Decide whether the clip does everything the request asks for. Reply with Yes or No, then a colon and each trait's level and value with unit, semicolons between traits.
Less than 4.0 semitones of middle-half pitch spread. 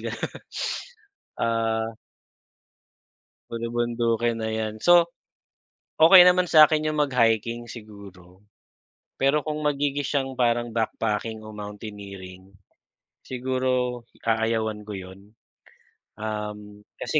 Yes: average, 3.6 semitones